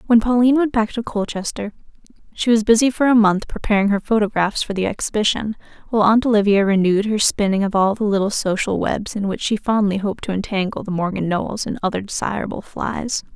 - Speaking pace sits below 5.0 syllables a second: No, 6.1 syllables/s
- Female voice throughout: Yes, female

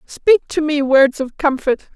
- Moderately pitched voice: No, very high, 290 Hz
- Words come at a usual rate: Yes, average, 185 wpm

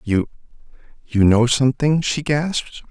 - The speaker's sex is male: Yes, male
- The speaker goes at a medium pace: No, slow, 105 wpm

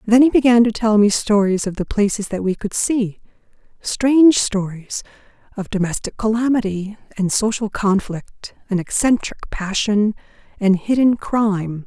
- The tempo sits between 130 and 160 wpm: Yes, slow, 135 wpm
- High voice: Yes, high, 210 Hz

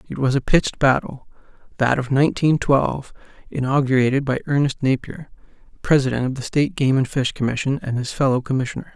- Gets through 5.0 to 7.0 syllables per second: Yes, 6.2 syllables/s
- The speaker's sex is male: Yes, male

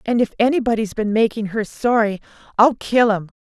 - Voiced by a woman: Yes, female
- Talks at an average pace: Yes, average, 175 wpm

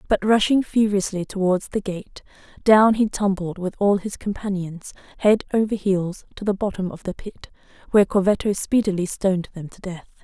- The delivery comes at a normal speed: Yes, average, 170 wpm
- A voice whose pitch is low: No, high, 195 Hz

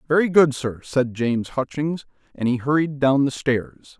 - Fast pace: No, average, 180 wpm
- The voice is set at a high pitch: No, low, 135 Hz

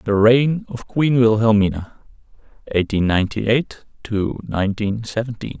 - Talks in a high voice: No, low, 110 Hz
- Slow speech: Yes, slow, 120 wpm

